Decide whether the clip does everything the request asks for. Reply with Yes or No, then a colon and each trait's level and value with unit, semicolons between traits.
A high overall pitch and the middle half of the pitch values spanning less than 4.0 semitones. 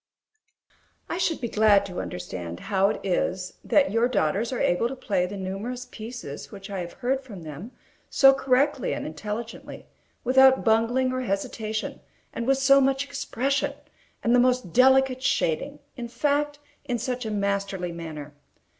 No: high, 230 Hz; average, 5.1 semitones